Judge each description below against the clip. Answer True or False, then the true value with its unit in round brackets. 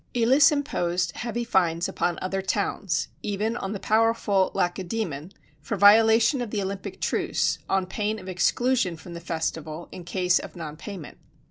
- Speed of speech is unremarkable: True (155 wpm)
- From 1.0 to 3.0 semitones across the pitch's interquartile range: False (4.3 semitones)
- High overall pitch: True (195 Hz)